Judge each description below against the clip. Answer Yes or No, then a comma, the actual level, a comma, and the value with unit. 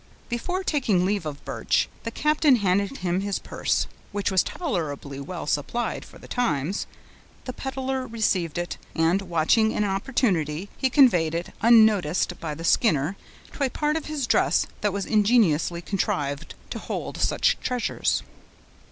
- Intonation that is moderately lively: No, wide, 6.6 semitones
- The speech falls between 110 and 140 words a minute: No, average, 150 wpm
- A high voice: Yes, high, 200 Hz